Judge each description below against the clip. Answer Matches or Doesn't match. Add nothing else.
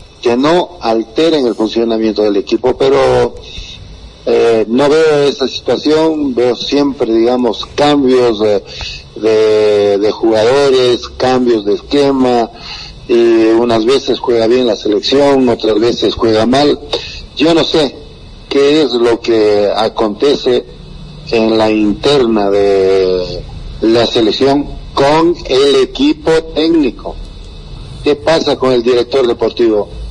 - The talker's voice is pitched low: Matches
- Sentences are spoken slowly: Matches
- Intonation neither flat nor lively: Matches